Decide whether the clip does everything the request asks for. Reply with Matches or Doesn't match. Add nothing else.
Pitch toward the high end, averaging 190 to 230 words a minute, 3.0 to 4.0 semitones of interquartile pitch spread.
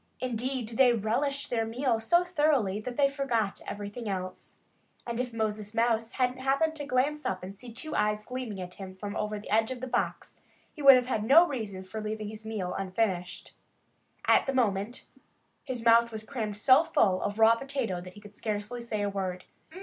Matches